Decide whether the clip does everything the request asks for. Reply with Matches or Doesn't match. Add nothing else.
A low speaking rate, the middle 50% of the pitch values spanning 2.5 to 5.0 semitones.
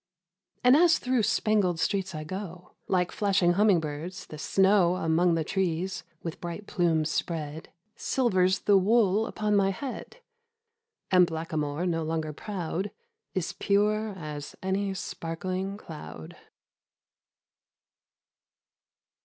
Matches